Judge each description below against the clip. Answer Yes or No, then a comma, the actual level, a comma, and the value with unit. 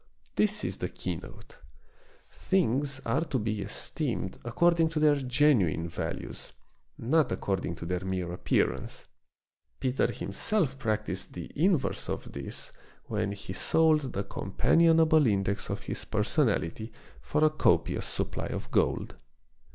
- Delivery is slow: Yes, slow, 130 wpm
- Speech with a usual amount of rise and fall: No, wide, 8.0 semitones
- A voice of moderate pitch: No, low, 125 Hz